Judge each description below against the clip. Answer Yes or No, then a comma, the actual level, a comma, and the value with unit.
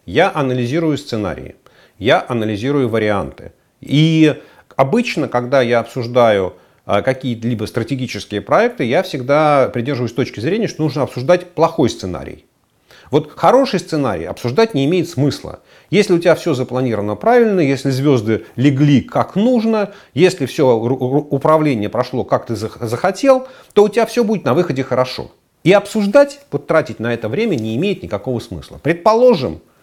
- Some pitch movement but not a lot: No, wide, 6.7 semitones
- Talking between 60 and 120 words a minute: No, average, 140 wpm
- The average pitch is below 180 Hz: Yes, medium, 140 Hz